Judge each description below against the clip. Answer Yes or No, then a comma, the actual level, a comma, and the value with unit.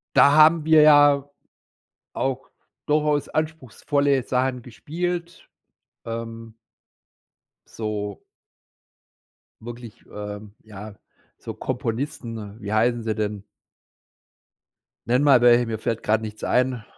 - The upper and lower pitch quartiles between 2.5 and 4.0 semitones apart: No, average, 4.7 semitones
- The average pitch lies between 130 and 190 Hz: No, low, 120 Hz